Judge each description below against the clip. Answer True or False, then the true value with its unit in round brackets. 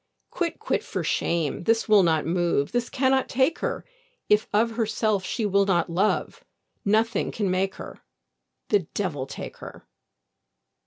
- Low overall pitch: False (205 Hz)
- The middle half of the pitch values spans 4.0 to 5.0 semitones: True (4.3 semitones)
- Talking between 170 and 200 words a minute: False (150 wpm)